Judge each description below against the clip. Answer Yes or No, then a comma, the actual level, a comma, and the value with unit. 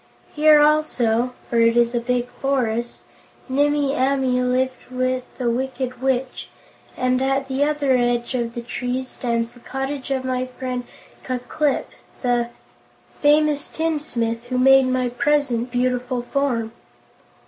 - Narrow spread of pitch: Yes, narrow, 1.9 semitones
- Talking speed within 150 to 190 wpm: No, slow, 135 wpm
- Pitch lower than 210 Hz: No, very high, 255 Hz